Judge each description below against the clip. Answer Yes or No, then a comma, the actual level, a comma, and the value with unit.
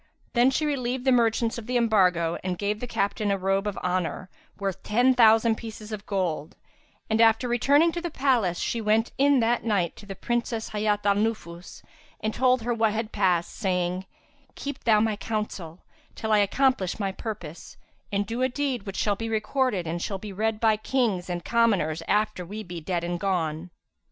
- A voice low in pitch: No, high, 215 Hz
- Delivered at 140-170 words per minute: No, average, 190 wpm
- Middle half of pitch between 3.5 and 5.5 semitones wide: Yes, average, 3.8 semitones